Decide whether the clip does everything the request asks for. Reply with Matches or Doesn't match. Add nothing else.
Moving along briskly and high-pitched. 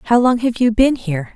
Matches